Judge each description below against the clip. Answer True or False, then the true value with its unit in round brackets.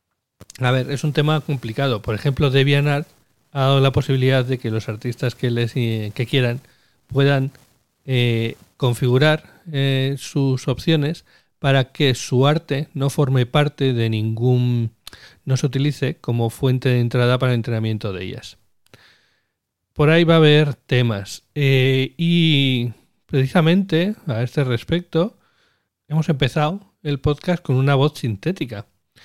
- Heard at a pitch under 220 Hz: True (135 Hz)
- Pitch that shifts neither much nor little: True (3.4 semitones)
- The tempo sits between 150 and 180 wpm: False (140 wpm)